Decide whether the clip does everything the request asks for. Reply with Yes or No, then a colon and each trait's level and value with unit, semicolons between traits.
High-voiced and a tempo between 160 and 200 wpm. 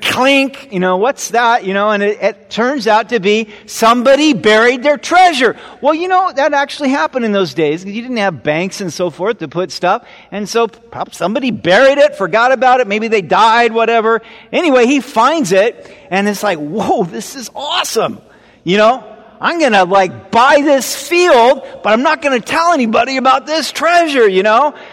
Yes: high, 230 Hz; average, 195 wpm